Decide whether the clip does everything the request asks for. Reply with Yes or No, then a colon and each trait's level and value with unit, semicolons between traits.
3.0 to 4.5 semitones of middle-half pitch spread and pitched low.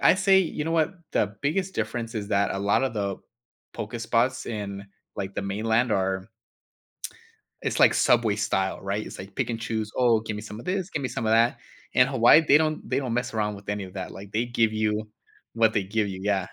Yes: average, 3.3 semitones; low, 110 Hz